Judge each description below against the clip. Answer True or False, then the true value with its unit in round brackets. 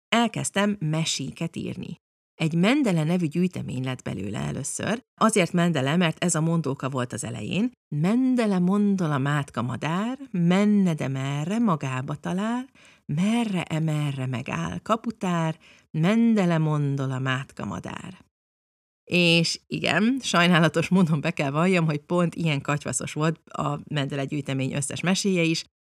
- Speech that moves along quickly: False (130 wpm)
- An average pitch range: True (5.0 semitones)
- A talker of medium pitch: True (165 Hz)